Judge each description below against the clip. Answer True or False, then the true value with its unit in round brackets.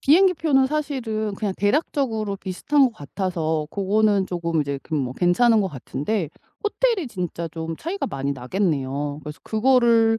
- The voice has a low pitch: False (200 Hz)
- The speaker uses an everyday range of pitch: False (7.5 semitones)